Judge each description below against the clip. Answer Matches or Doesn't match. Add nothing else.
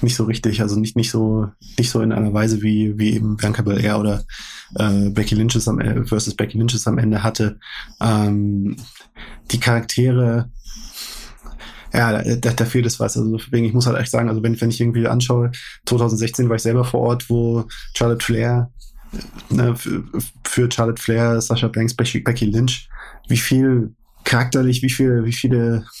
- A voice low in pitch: Matches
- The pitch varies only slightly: Matches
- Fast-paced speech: Doesn't match